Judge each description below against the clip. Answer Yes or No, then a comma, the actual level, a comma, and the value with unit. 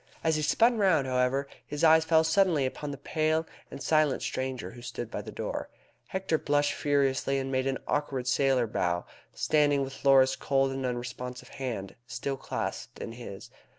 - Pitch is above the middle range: No, low, 135 Hz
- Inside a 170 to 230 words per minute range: Yes, average, 175 wpm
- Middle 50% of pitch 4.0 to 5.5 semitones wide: No, average, 3.1 semitones